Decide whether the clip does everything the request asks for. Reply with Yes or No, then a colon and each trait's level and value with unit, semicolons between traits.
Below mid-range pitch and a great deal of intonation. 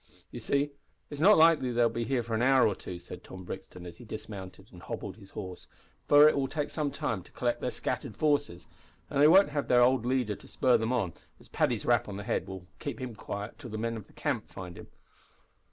Yes: low, 120 Hz; wide, 5.7 semitones